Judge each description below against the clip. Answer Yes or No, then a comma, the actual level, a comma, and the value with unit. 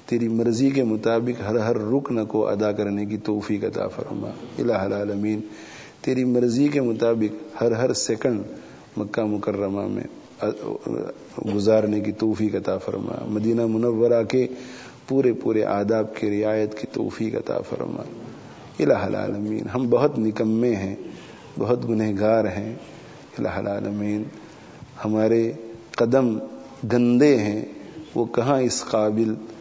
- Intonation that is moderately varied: No, narrow, 2.2 semitones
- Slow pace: Yes, slow, 125 wpm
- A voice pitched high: No, low, 110 Hz